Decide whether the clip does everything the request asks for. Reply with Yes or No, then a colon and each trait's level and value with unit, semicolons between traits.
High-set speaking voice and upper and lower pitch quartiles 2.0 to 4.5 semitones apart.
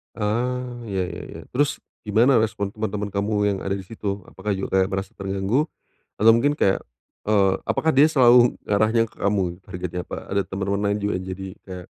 No: low, 105 Hz; average, 2.9 semitones